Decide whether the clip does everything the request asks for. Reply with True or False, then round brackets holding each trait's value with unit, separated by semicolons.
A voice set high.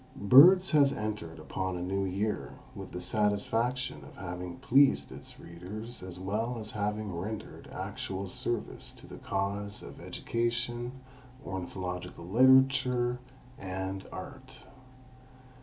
False (105 Hz)